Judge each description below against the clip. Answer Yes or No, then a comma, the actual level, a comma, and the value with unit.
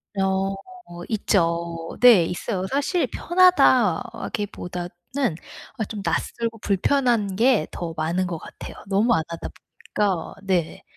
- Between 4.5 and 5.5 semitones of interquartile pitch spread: Yes, average, 5.1 semitones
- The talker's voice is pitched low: No, high, 195 Hz